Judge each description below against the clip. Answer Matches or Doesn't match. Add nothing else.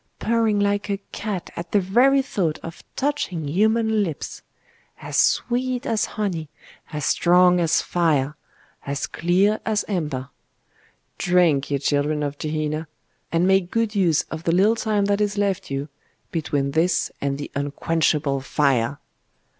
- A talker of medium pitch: Matches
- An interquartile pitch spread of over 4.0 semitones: Matches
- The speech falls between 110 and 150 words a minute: Matches